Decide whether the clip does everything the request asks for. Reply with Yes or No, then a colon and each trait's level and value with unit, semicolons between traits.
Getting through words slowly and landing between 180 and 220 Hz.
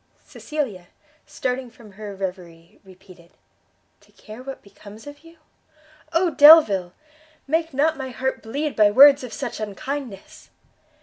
No: slow, 130 wpm; very high, 250 Hz